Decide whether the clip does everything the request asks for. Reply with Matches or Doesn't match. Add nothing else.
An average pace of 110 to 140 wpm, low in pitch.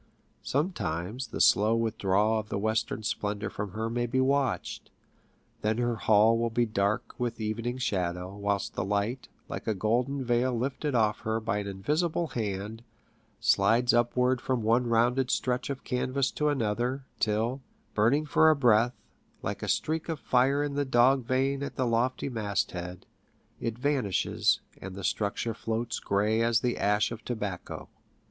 Doesn't match